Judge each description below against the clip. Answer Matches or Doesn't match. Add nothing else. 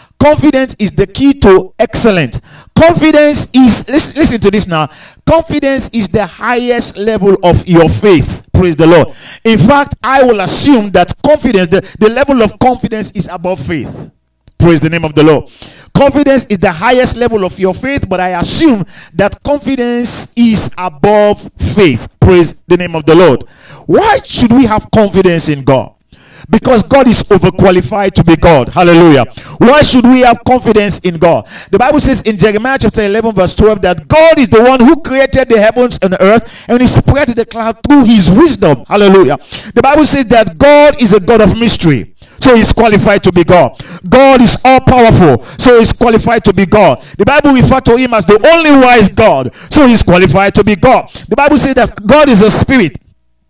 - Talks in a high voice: Matches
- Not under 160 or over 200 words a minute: Matches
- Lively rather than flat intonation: Matches